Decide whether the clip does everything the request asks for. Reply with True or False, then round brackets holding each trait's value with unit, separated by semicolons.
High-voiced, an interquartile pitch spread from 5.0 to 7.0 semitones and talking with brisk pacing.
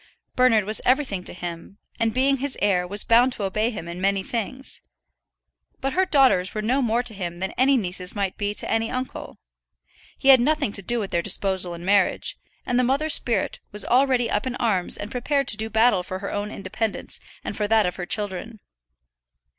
False (220 Hz; 4.6 semitones; 210 wpm)